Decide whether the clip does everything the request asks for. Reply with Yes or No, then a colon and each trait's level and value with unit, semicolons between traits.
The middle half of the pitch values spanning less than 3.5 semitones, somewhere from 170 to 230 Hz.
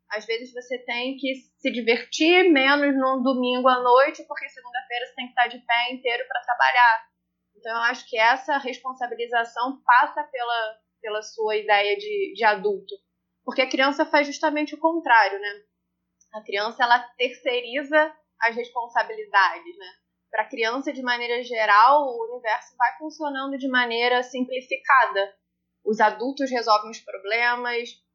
No: average, 2.9 semitones; high, 245 Hz